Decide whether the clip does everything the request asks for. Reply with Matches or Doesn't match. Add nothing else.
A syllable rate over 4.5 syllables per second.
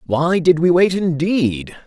Doesn't match